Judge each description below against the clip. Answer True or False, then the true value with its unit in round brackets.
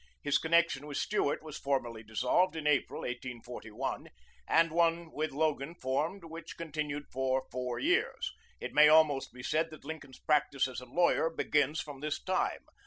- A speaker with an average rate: True (165 wpm)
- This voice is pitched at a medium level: True (150 Hz)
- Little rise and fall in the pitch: False (3.5 semitones)